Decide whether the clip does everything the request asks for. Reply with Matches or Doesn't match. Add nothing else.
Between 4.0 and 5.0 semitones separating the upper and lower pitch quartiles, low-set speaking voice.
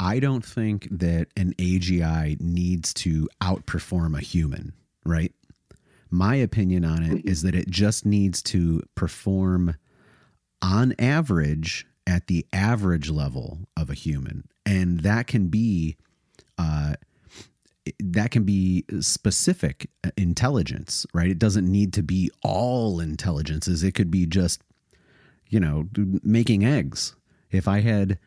Doesn't match